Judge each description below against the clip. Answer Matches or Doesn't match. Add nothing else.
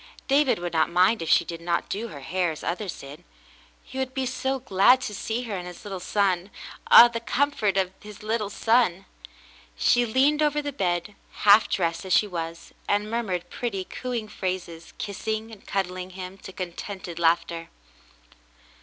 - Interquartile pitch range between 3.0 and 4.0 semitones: Doesn't match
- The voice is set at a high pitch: Matches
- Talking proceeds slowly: Doesn't match